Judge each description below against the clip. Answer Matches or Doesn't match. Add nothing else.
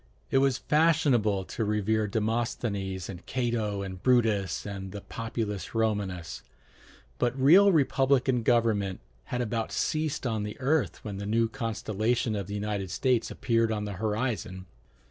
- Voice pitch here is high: Doesn't match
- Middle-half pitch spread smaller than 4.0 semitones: Matches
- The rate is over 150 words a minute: Doesn't match